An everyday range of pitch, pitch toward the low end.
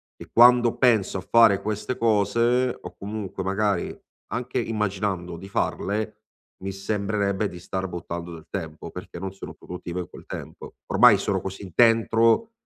Yes: average, 3.3 semitones; low, 100 Hz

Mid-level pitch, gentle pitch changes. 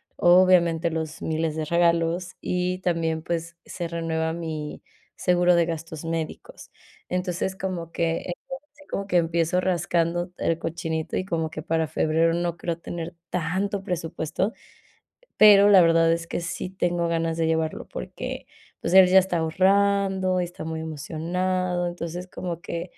Yes: medium, 170 Hz; narrow, 1.9 semitones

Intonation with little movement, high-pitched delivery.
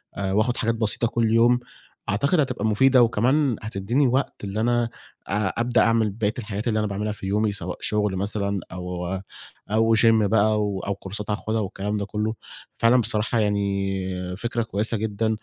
No: narrow, 2.3 semitones; low, 110 Hz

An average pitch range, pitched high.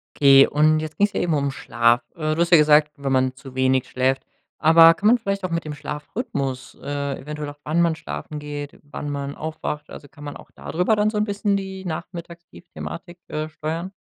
No: average, 3.3 semitones; medium, 150 Hz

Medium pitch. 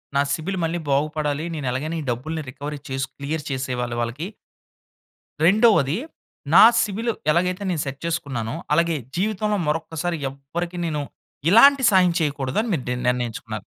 Yes: medium, 155 Hz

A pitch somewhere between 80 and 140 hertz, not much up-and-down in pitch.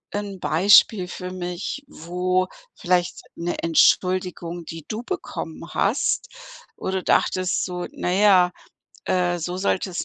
No: medium, 180 Hz; narrow, 1.3 semitones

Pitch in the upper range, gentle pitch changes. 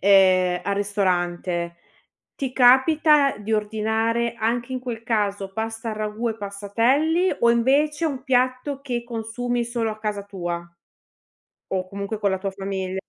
No: high, 220 Hz; average, 3.7 semitones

